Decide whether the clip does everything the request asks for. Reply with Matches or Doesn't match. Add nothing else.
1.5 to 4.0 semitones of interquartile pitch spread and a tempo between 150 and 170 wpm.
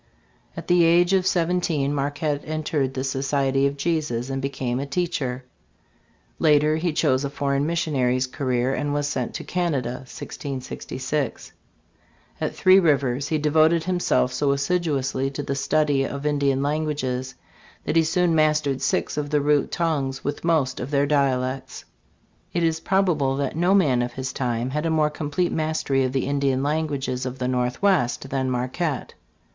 Matches